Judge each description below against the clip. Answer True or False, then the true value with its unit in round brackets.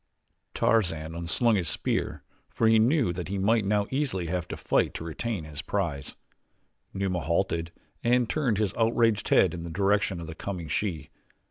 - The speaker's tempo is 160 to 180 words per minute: True (175 wpm)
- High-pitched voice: False (95 Hz)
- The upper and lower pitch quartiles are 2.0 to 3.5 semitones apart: False (5.0 semitones)